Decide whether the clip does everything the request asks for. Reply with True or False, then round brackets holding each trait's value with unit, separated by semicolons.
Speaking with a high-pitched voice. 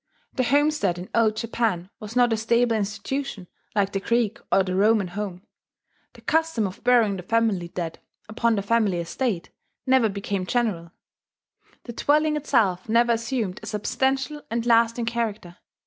True (225 Hz)